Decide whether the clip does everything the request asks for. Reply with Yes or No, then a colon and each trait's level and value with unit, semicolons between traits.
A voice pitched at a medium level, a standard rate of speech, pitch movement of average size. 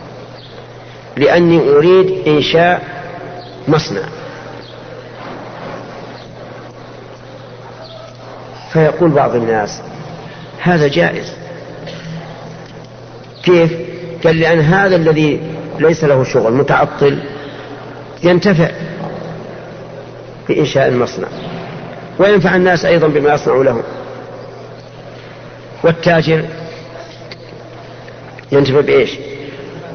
No: medium, 160 Hz; slow, 60 wpm; average, 3.7 semitones